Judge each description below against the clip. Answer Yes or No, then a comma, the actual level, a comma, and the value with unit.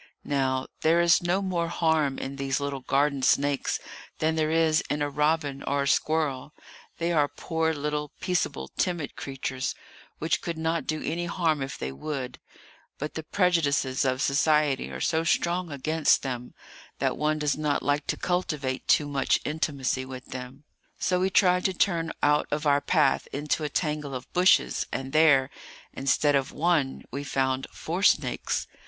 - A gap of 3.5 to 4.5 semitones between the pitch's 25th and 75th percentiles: No, average, 2.9 semitones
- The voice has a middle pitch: Yes, medium, 150 Hz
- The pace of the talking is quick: No, average, 165 wpm